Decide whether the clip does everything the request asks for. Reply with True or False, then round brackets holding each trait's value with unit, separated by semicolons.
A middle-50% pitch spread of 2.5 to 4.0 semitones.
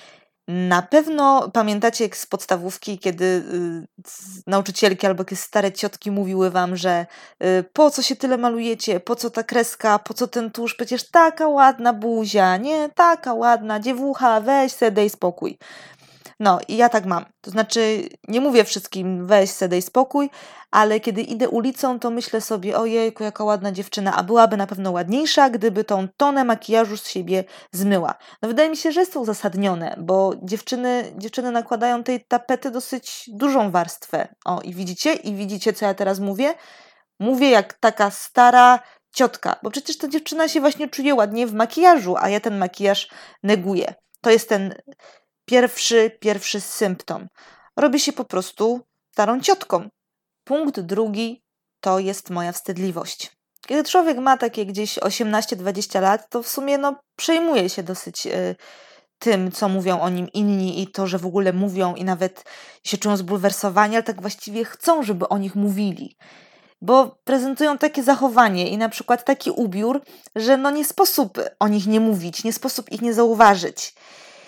False (4.6 semitones)